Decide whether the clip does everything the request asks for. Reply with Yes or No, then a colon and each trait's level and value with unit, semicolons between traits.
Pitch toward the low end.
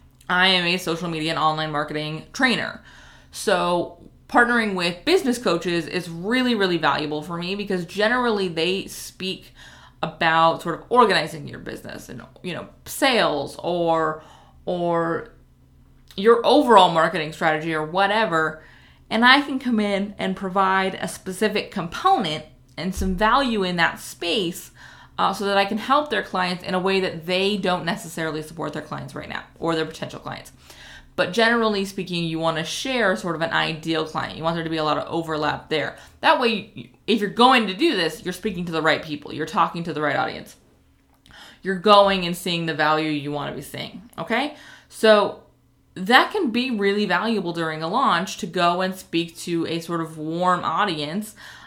No: medium, 175 Hz